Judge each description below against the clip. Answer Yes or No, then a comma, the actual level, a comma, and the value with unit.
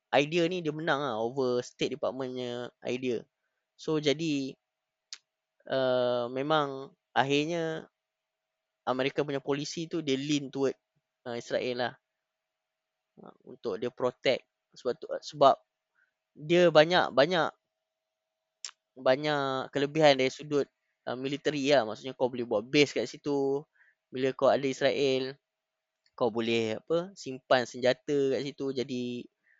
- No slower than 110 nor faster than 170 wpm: Yes, average, 120 wpm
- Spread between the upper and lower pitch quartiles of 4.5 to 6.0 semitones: No, average, 3.8 semitones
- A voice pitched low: Yes, low, 130 Hz